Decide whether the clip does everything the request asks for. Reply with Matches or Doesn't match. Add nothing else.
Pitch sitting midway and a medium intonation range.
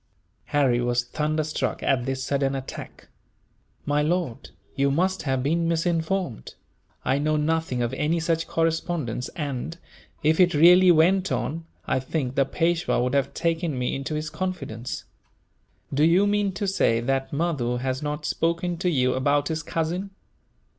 Matches